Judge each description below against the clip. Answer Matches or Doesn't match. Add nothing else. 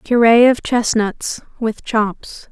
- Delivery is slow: Matches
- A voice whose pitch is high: Matches